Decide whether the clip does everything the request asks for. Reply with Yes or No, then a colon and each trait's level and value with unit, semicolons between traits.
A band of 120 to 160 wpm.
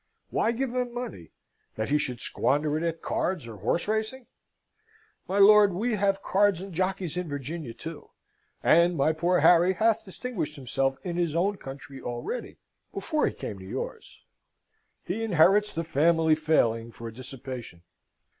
Yes: average, 155 wpm